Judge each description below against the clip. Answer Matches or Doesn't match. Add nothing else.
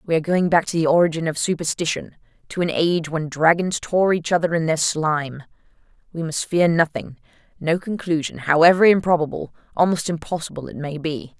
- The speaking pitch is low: Doesn't match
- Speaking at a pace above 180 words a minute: Doesn't match